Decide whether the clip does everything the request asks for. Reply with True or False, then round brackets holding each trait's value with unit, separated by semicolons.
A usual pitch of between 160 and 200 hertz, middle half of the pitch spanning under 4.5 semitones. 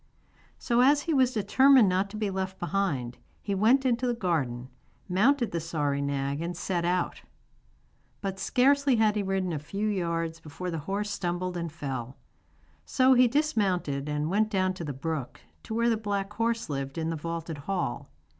False (185 Hz; 5.4 semitones)